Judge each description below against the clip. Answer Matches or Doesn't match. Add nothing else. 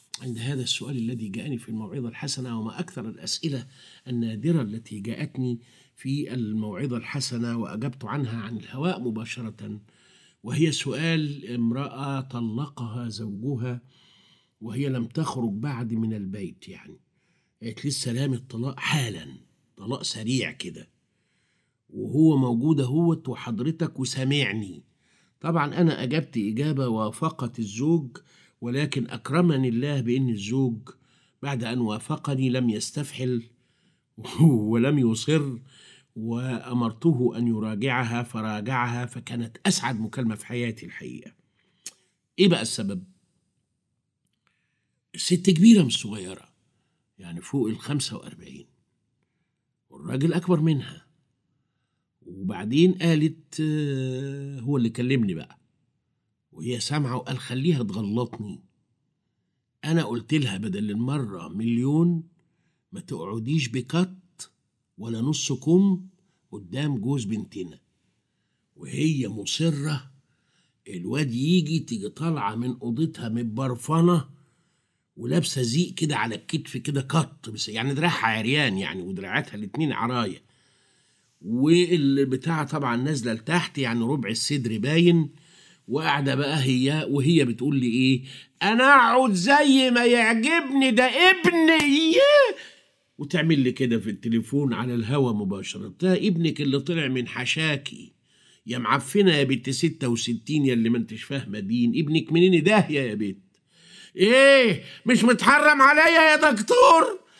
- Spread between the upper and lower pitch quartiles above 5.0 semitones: Matches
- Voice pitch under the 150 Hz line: Matches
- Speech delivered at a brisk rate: Doesn't match